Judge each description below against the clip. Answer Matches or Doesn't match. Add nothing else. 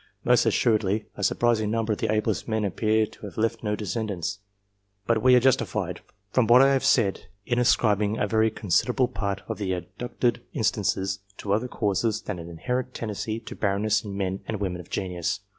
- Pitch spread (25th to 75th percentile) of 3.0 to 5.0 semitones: Doesn't match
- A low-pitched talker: Matches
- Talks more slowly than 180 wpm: Doesn't match